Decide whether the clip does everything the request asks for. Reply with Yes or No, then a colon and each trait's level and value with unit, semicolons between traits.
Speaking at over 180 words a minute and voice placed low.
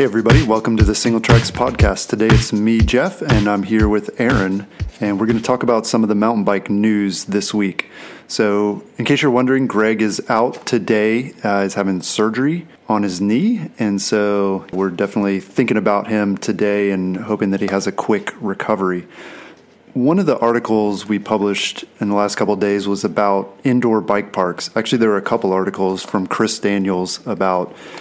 Yes: average, 190 wpm; low, 105 Hz